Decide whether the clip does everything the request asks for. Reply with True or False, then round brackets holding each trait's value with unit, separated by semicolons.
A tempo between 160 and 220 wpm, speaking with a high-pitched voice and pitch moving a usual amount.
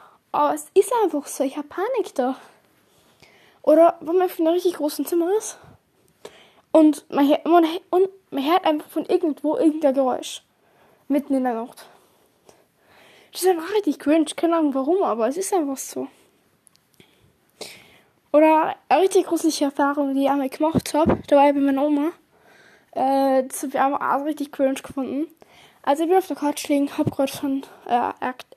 True (170 wpm; 300 Hz; 3.5 semitones)